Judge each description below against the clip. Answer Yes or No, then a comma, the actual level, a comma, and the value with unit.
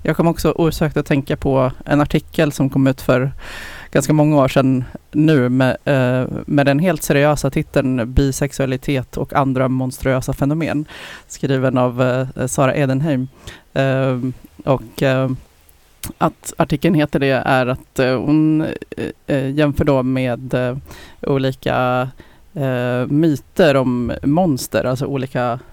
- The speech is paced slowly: Yes, slow, 115 wpm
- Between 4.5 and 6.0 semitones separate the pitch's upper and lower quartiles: No, narrow, 2.4 semitones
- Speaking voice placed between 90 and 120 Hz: No, low, 135 Hz